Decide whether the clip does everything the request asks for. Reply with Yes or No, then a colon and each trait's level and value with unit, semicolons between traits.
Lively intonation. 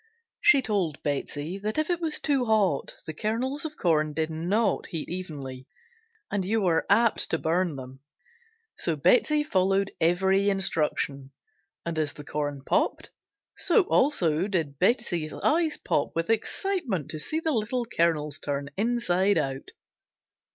Yes: wide, 7.0 semitones